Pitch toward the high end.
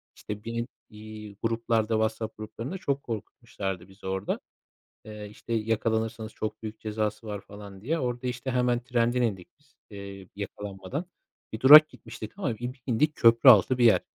No: low, 110 Hz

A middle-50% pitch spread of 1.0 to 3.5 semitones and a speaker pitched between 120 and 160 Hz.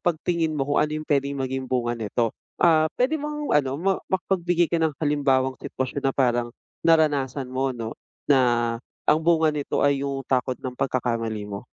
No: average, 3.9 semitones; medium, 140 Hz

